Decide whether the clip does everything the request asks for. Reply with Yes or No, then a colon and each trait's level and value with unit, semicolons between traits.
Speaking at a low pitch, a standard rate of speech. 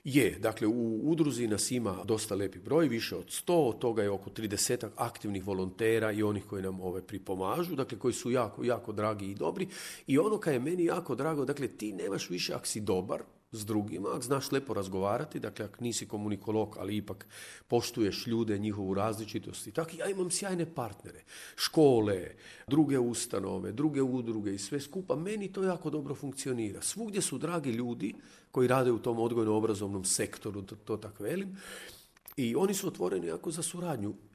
No: low, 115 Hz; fast, 180 wpm